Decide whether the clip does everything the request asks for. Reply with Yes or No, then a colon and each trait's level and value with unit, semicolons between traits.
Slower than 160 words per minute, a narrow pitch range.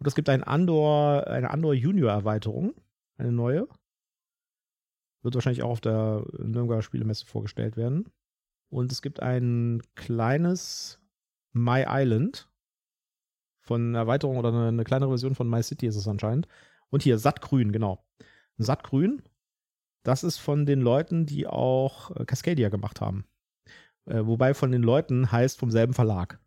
No: average, 140 wpm; average, 3.8 semitones